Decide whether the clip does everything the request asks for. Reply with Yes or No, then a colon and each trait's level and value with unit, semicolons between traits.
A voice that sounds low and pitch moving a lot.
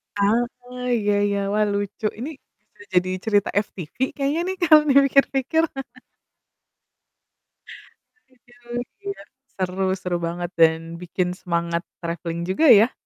No: high, 205 Hz; wide, 7.1 semitones